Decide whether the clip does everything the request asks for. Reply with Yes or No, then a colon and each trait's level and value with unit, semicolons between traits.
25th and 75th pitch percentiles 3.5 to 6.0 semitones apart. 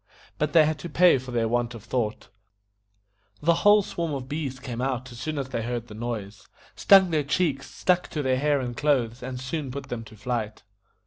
Yes: average, 4.1 semitones